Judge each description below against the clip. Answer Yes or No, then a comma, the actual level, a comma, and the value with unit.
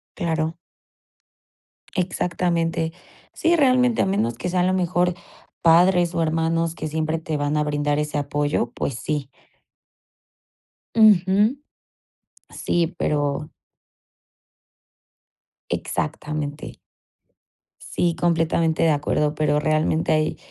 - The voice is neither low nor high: Yes, medium, 160 Hz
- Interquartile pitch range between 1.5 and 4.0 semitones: Yes, average, 2.8 semitones